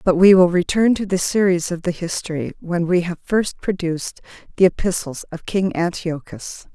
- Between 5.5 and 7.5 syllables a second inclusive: No, 5.0 syllables/s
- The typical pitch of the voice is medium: Yes, medium, 175 Hz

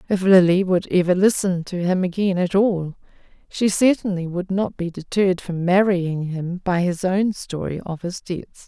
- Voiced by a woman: Yes, female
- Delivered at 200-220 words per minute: No, average, 180 wpm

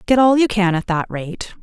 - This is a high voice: Yes, high, 205 Hz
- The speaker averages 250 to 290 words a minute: Yes, fast, 260 wpm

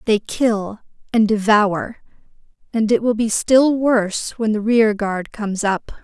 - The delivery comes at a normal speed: Yes, average, 150 wpm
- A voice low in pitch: No, high, 220 Hz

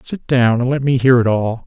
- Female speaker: No, male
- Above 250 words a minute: Yes, fast, 290 wpm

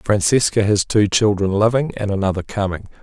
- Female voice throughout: No, male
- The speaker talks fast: No, average, 160 wpm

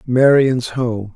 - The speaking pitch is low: Yes, low, 125 Hz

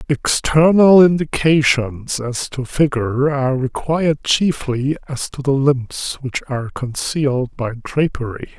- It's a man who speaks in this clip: Yes, male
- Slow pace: Yes, slow, 120 wpm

